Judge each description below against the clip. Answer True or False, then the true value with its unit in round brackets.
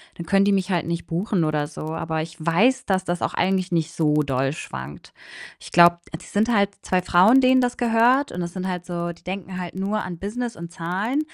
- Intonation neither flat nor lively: True (3.4 semitones)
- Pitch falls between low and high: True (180 Hz)